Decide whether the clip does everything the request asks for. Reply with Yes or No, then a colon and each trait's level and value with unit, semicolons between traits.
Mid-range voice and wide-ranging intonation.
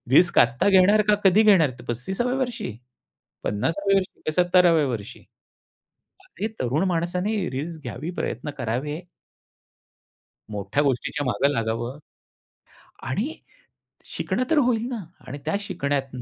Yes: medium, 165 Hz; wide, 7.5 semitones